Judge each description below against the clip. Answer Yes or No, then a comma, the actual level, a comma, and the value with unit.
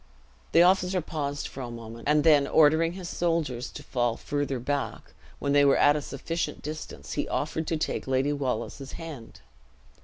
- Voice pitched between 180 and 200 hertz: No, medium, 145 Hz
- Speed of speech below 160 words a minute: No, average, 175 wpm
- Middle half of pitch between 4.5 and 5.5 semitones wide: No, average, 3.2 semitones